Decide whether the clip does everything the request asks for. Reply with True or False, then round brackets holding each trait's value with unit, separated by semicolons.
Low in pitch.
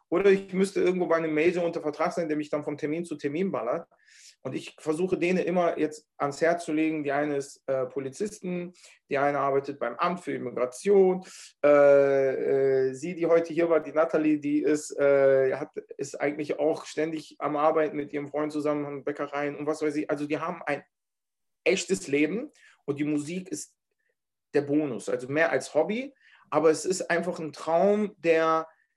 False (155 Hz)